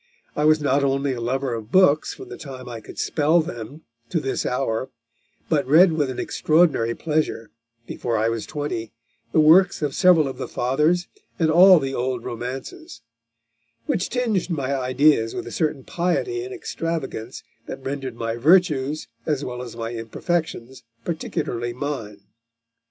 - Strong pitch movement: No, average, 4.7 semitones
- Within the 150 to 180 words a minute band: Yes, average, 160 wpm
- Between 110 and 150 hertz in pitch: Yes, medium, 140 Hz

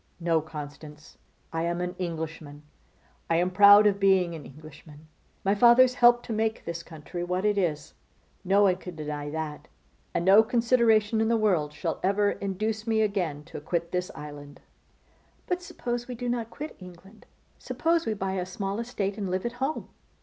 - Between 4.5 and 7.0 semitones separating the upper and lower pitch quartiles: Yes, average, 5.2 semitones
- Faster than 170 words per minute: Yes, average, 180 wpm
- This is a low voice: No, high, 190 Hz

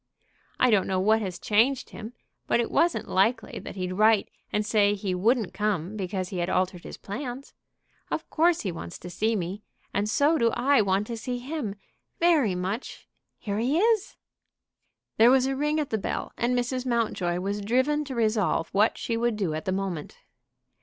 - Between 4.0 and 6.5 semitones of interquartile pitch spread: Yes, average, 4.7 semitones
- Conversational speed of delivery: Yes, average, 190 wpm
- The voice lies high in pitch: Yes, high, 215 Hz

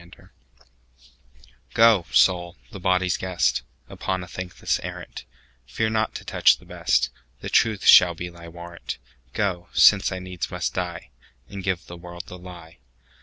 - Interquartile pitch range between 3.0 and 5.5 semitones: No, narrow, 2.6 semitones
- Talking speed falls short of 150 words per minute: Yes, slow, 135 wpm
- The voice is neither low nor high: No, very low, 90 Hz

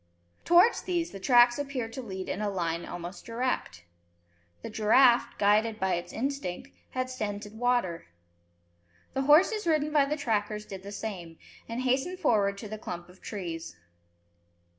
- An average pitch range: No, wide, 5.7 semitones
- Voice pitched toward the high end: Yes, high, 220 Hz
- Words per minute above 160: No, average, 155 wpm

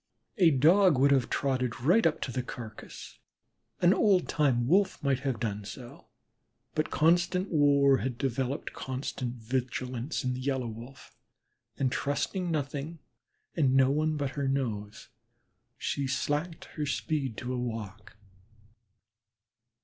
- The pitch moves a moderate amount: Yes, average, 3.5 semitones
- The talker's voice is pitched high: No, low, 135 Hz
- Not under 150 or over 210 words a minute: No, slow, 135 wpm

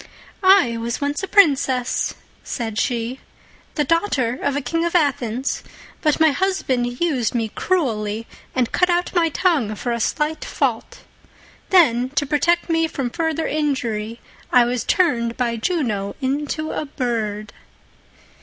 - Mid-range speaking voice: No, very high, 265 Hz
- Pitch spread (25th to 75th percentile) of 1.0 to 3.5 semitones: No, wide, 5.5 semitones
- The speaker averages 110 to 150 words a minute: Yes, average, 145 wpm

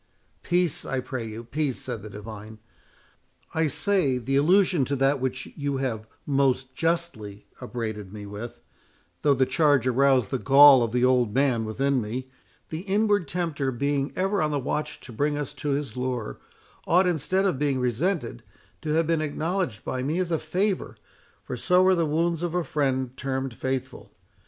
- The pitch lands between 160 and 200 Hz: No, medium, 140 Hz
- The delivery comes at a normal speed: Yes, average, 170 wpm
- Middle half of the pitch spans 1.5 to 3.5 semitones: No, average, 4.4 semitones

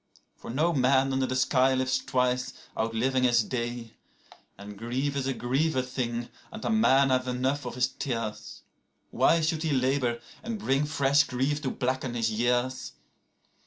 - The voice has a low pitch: Yes, low, 130 Hz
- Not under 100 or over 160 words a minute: Yes, average, 155 wpm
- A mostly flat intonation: Yes, narrow, 2.1 semitones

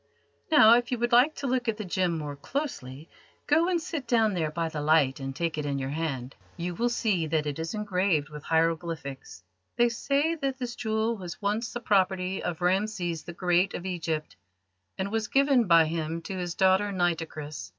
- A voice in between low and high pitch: Yes, medium, 180 Hz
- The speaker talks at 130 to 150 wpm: No, average, 200 wpm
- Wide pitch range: Yes, wide, 5.9 semitones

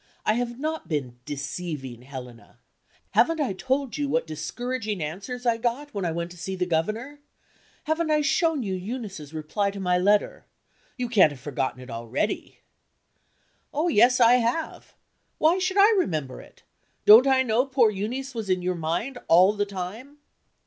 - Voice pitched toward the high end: Yes, high, 210 Hz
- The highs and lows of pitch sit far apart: Yes, wide, 7.4 semitones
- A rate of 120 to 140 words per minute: No, average, 170 wpm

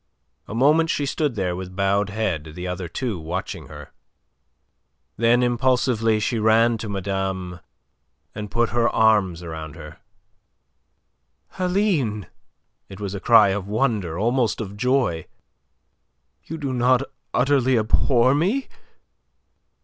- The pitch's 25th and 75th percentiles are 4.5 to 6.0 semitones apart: Yes, average, 5.0 semitones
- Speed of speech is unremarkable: No, slow, 125 wpm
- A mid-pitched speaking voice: No, low, 110 Hz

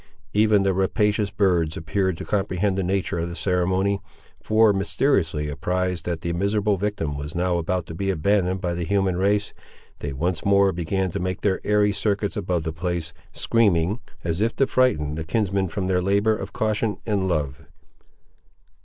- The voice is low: Yes, very low, 95 Hz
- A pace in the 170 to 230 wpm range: Yes, average, 175 wpm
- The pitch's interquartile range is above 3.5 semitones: No, average, 3.1 semitones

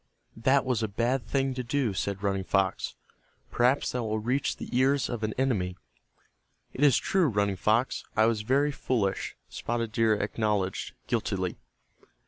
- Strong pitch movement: No, average, 4.2 semitones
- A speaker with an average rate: Yes, average, 155 wpm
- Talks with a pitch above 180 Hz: No, low, 115 Hz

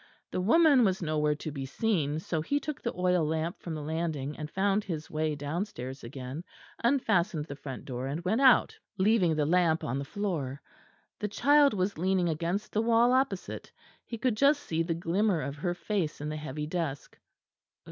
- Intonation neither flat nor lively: No, wide, 5.7 semitones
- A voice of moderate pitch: Yes, medium, 170 Hz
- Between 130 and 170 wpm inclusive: No, average, 190 wpm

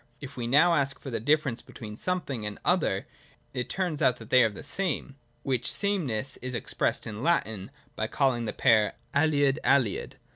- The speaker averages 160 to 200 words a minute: Yes, average, 180 wpm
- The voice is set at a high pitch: No, low, 130 Hz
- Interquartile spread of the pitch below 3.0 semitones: No, average, 4.5 semitones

